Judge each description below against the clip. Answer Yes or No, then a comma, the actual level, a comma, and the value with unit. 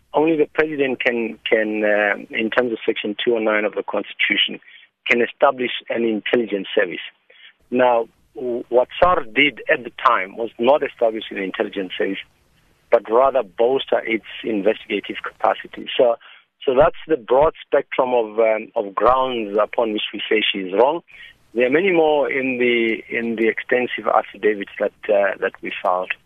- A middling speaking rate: Yes, average, 160 wpm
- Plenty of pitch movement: No, average, 3.3 semitones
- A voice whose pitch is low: Yes, low, 115 Hz